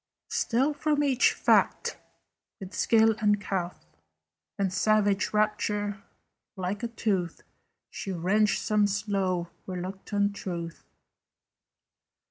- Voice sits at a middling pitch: No, high, 205 Hz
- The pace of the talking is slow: Yes, slow, 95 wpm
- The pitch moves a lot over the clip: No, narrow, 2.4 semitones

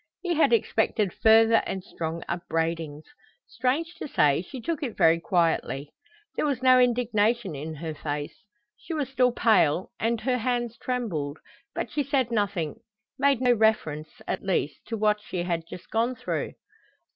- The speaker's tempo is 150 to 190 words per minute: Yes, average, 160 wpm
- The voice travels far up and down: Yes, wide, 7.3 semitones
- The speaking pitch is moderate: No, high, 220 Hz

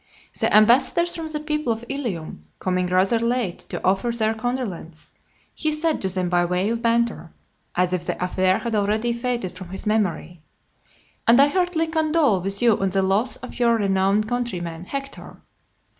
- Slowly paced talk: No, average, 175 wpm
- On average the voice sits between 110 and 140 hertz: No, high, 220 Hz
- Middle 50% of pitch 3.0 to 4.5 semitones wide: No, average, 5.2 semitones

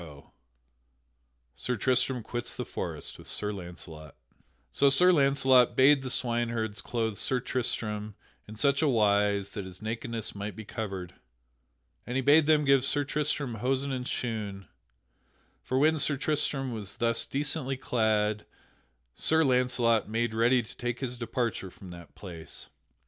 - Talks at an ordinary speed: Yes, average, 150 wpm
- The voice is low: Yes, low, 120 Hz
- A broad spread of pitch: No, average, 4.2 semitones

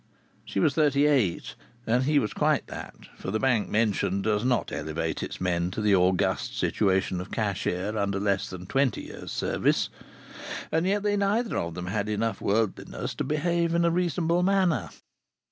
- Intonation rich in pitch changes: Yes, wide, 8.7 semitones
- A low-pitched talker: Yes, low, 110 Hz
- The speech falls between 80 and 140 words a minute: No, average, 175 wpm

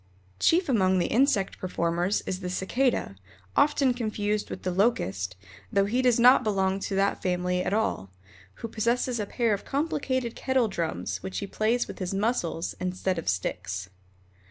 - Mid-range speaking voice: No, high, 200 Hz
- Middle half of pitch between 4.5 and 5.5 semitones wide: Yes, average, 4.9 semitones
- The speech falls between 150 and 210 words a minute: Yes, average, 165 wpm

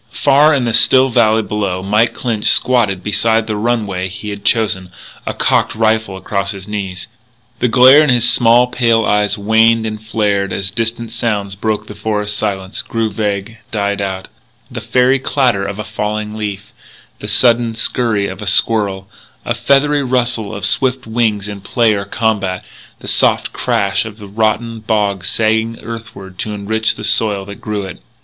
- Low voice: Yes, low, 110 Hz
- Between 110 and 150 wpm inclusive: No, average, 170 wpm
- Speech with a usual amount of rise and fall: No, narrow, 2.3 semitones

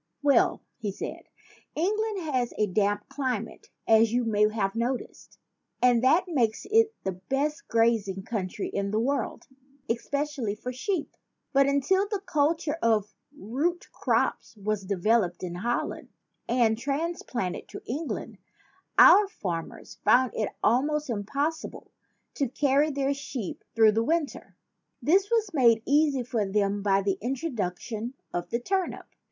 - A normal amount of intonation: No, wide, 5.8 semitones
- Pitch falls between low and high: No, high, 245 Hz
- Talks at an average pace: Yes, average, 145 wpm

